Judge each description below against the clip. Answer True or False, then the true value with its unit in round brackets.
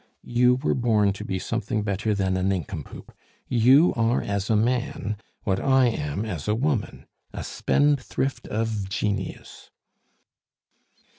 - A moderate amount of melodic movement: True (3.9 semitones)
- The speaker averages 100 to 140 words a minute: True (135 wpm)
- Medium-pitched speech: False (110 Hz)